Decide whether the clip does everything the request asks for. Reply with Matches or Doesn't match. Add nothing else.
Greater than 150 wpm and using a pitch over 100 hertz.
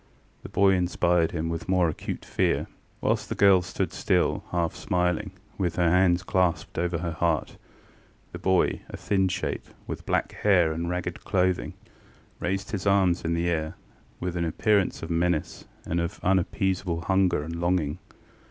Doesn't match